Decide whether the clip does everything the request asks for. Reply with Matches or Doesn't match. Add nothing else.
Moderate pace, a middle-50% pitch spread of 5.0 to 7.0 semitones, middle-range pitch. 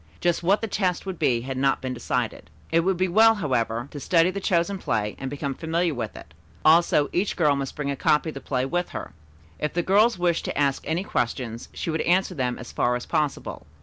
Doesn't match